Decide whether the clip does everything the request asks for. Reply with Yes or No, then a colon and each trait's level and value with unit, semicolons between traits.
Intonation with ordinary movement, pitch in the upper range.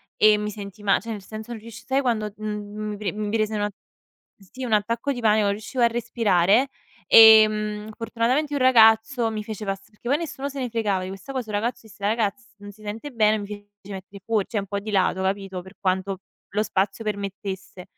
No: narrow, 2.2 semitones; high, 215 Hz